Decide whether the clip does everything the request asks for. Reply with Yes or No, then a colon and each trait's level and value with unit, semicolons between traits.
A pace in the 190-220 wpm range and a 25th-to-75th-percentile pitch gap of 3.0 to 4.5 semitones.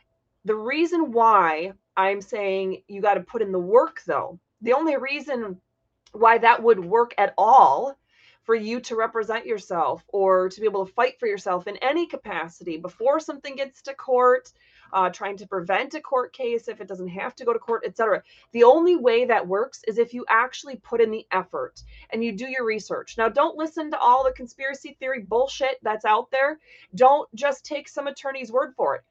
No: average, 200 wpm; wide, 5.4 semitones